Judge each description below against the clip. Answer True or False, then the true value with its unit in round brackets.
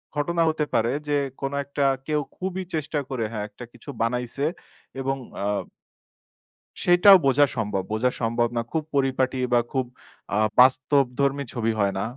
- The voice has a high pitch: False (135 Hz)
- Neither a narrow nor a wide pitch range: True (3.7 semitones)